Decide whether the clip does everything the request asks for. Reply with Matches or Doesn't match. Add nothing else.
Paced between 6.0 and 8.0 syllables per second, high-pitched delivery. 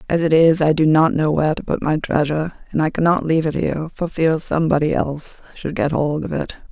Doesn't match